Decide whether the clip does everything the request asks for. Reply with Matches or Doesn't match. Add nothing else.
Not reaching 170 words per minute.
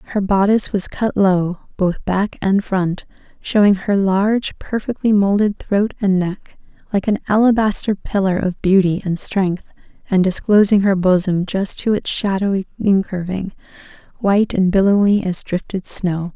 Matches